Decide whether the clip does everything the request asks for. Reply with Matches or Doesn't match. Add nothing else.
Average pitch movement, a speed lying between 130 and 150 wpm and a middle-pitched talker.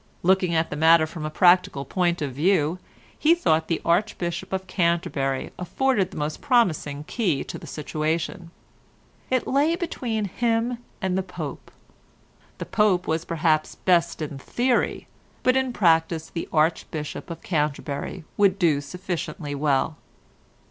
Matches